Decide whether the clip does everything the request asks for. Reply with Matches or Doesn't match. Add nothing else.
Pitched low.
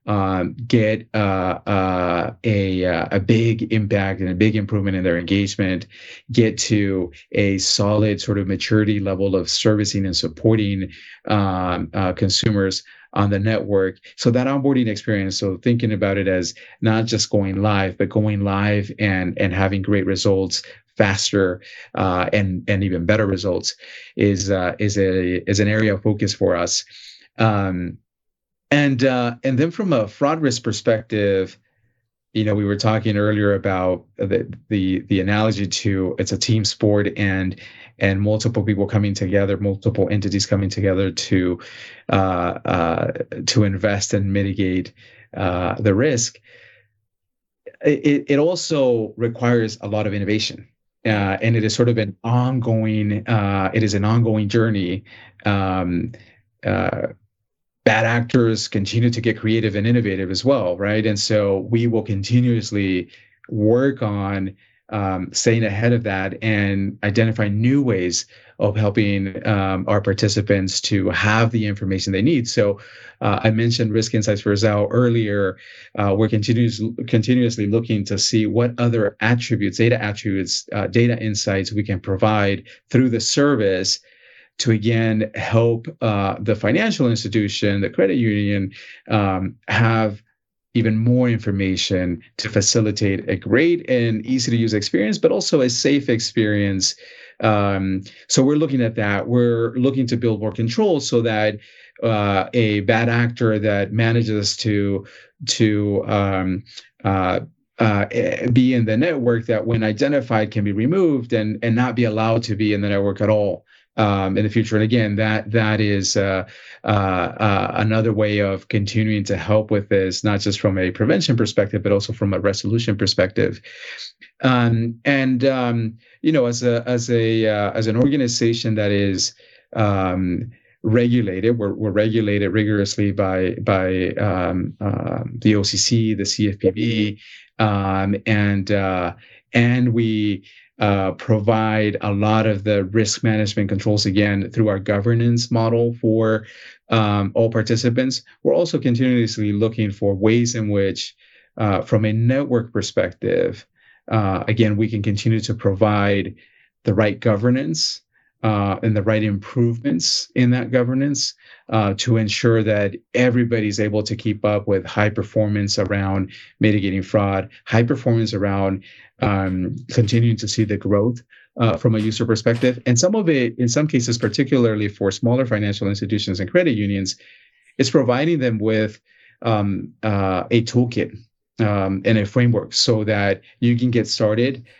Matches